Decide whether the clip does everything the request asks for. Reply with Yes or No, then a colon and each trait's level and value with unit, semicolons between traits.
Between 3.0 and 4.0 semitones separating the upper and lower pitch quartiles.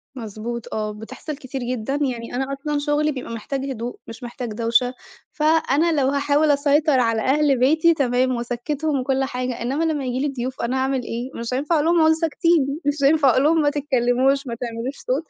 Yes: average, 3.3 semitones